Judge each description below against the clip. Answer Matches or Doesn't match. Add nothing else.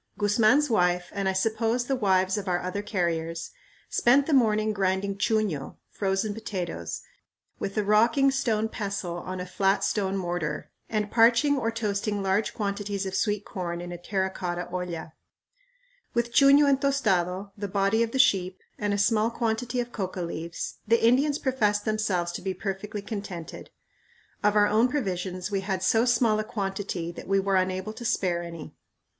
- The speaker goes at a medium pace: Matches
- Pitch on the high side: Matches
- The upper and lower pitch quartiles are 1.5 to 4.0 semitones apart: Matches